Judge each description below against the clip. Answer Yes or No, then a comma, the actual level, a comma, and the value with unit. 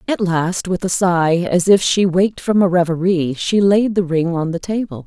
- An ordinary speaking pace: No, fast, 225 wpm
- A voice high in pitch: No, medium, 180 Hz